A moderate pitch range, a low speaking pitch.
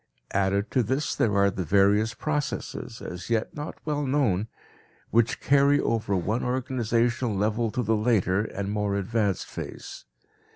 Yes: average, 4.0 semitones; low, 110 Hz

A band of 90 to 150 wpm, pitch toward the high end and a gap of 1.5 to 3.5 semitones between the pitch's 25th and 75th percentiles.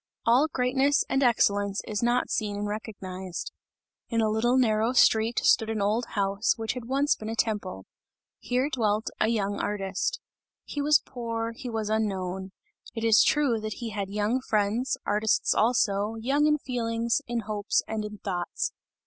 No: average, 165 wpm; high, 220 Hz; average, 2.9 semitones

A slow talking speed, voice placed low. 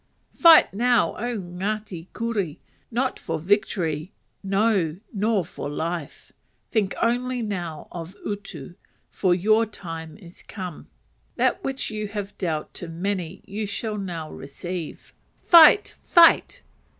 No: slow, 125 wpm; high, 195 Hz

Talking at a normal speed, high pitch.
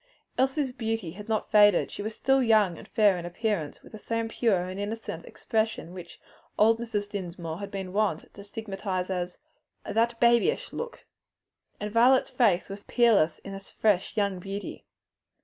Yes: average, 170 wpm; high, 205 Hz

